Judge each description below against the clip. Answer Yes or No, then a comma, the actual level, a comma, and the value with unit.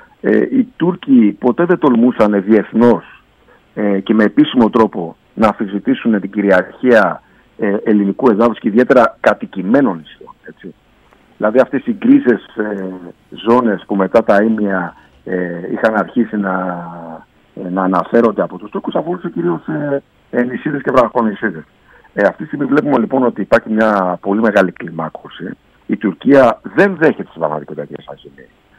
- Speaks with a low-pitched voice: Yes, low, 105 Hz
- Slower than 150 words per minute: Yes, average, 135 wpm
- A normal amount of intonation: Yes, average, 4.4 semitones